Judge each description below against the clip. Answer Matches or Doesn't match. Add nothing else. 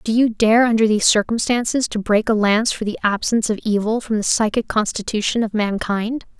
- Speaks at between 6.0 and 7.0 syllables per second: Doesn't match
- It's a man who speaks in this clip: Doesn't match